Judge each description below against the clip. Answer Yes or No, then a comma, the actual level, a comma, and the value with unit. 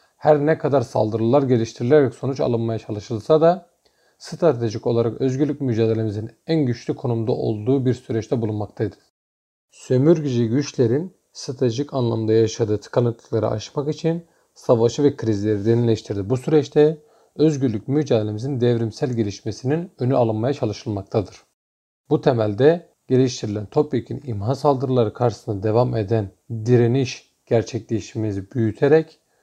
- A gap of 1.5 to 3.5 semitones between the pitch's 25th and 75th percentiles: No, average, 4.4 semitones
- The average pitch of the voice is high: No, low, 120 Hz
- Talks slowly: Yes, slow, 110 wpm